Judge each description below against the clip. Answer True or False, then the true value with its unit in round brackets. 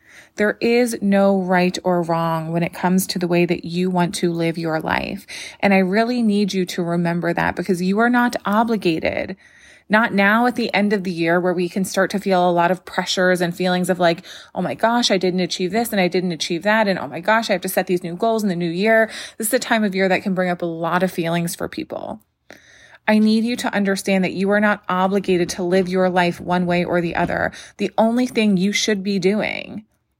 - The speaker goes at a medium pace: False (245 wpm)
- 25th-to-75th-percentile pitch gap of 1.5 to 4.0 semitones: True (3.0 semitones)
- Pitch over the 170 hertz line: True (185 Hz)